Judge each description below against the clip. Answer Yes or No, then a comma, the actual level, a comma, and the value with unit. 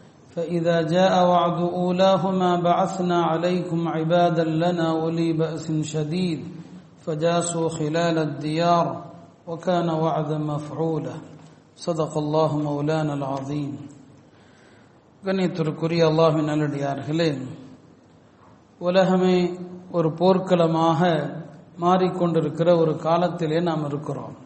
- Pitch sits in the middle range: Yes, medium, 165 Hz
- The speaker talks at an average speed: Yes, average, 90 wpm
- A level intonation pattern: Yes, narrow, 2.1 semitones